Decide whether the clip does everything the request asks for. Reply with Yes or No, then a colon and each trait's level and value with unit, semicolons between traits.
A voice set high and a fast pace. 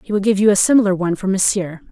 Yes: high, 195 Hz; fast, 285 wpm